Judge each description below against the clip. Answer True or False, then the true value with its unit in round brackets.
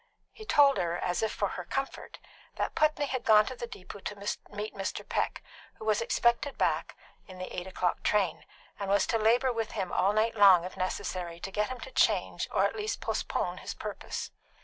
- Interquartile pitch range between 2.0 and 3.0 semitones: False (4.2 semitones)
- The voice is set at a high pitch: True (210 Hz)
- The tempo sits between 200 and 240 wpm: True (205 wpm)